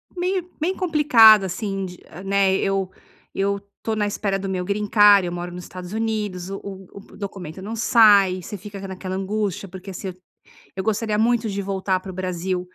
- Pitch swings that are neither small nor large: No, narrow, 2.3 semitones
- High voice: Yes, high, 195 Hz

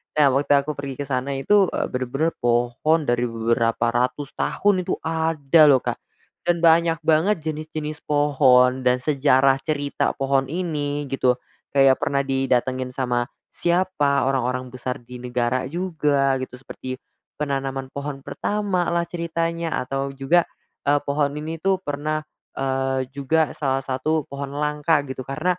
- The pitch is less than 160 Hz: Yes, medium, 140 Hz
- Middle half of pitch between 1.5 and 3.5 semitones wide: Yes, average, 3.2 semitones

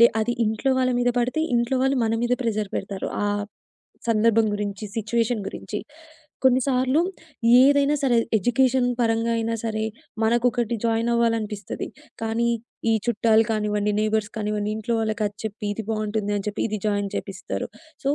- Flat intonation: Yes, narrow, 2.2 semitones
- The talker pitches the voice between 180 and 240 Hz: Yes, high, 225 Hz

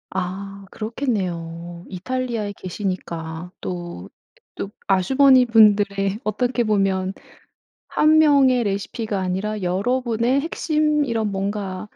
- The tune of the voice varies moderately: Yes, average, 4.8 semitones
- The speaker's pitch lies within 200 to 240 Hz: Yes, high, 205 Hz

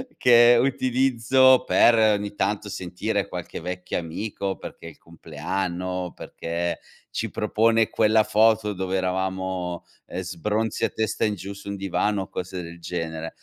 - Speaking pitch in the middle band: No, low, 100 Hz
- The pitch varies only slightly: No, average, 3.5 semitones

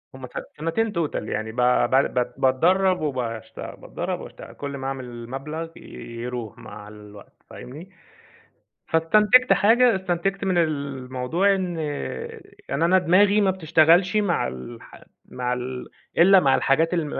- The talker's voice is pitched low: No, medium, 155 Hz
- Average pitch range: No, wide, 6.7 semitones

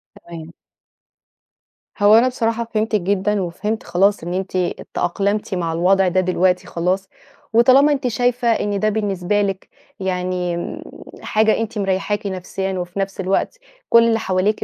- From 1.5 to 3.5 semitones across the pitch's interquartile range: Yes, average, 3.0 semitones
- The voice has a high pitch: Yes, high, 195 Hz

